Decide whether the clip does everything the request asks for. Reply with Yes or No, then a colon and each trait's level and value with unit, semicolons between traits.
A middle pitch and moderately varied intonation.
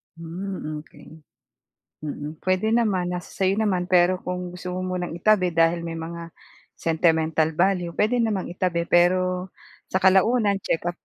No: medium, 180 Hz; narrow, 2.2 semitones